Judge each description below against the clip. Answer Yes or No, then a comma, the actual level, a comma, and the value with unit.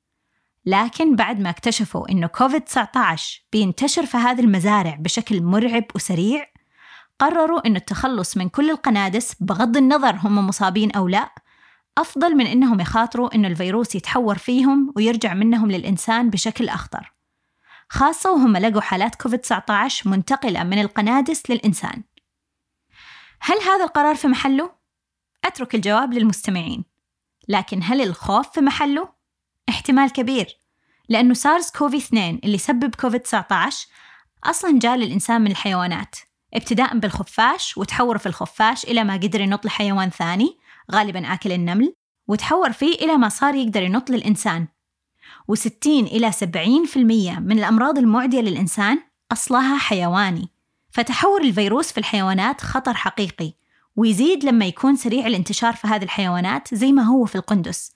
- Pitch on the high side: Yes, high, 225 Hz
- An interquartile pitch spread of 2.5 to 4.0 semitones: No, average, 4.6 semitones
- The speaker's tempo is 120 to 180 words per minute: Yes, average, 130 wpm